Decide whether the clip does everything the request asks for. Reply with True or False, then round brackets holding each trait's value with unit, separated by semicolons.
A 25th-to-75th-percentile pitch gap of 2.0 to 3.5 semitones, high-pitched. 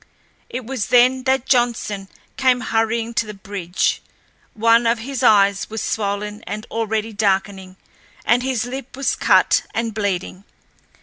True (3.2 semitones; 225 Hz)